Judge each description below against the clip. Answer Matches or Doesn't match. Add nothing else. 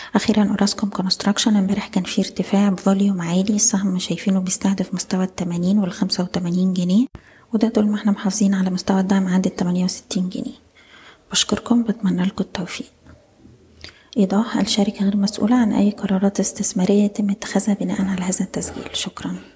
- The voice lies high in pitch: Matches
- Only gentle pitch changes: Matches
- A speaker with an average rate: Doesn't match